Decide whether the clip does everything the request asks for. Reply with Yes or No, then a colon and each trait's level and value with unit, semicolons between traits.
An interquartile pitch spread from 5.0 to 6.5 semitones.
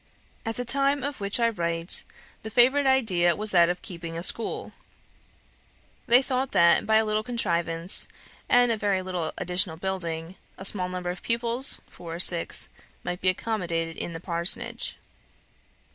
Yes: average, 5.3 semitones